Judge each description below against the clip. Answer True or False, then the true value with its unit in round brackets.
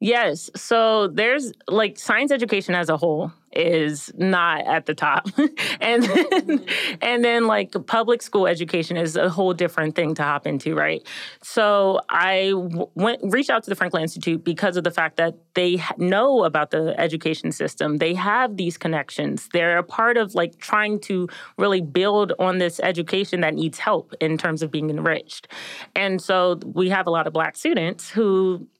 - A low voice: False (185 Hz)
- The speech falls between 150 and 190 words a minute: True (175 wpm)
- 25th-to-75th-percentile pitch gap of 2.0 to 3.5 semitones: False (4.1 semitones)